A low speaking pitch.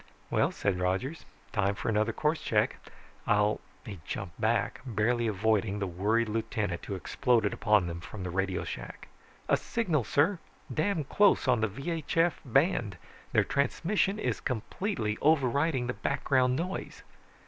Yes: low, 115 Hz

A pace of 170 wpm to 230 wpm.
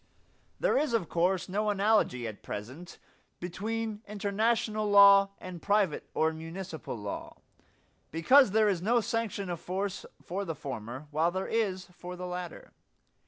No: average, 145 wpm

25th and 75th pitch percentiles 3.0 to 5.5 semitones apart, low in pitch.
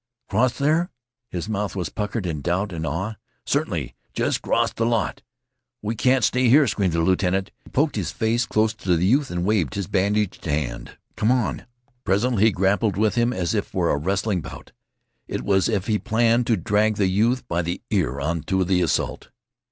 Yes: average, 4.2 semitones; low, 100 Hz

